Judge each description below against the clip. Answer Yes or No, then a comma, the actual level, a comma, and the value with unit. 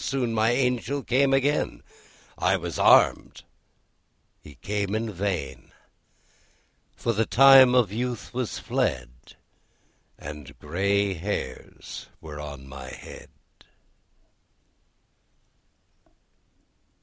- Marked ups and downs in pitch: Yes, wide, 8.8 semitones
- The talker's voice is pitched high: No, low, 100 Hz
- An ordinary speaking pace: No, slow, 90 wpm